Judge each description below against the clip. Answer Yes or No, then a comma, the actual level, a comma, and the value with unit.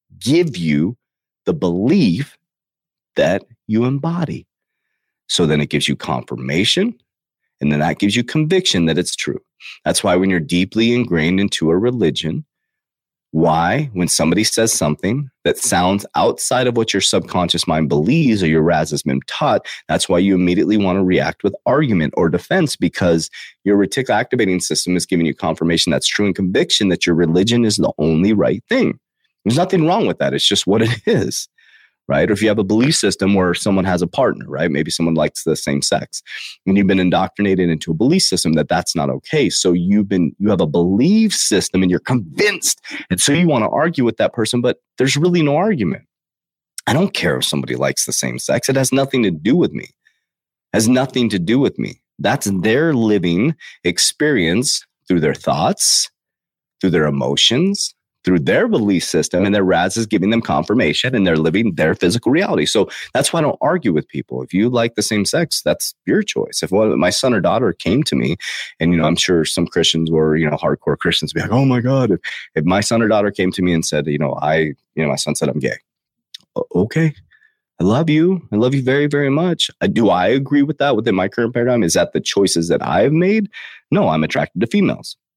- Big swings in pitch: Yes, wide, 6.6 semitones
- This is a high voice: No, very low, 95 Hz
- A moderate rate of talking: No, fast, 210 wpm